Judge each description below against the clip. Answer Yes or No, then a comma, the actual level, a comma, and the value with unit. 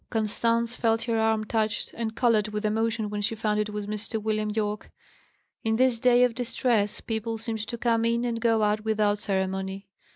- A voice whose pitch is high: Yes, high, 220 Hz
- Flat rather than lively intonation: Yes, narrow, 1.6 semitones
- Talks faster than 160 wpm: Yes, average, 190 wpm